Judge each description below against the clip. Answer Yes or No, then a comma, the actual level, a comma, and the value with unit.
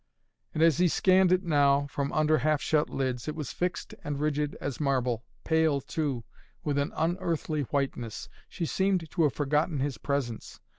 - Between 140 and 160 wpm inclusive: No, average, 170 wpm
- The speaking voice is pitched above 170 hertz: No, medium, 150 Hz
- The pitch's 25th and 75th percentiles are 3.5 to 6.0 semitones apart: No, narrow, 2.6 semitones